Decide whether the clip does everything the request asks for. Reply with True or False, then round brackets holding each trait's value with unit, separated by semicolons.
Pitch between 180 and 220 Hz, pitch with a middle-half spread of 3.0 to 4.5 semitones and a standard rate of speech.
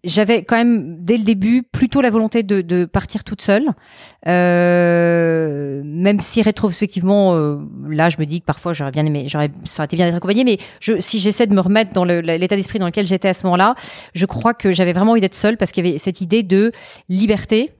False (190 Hz; 3.9 semitones; 230 wpm)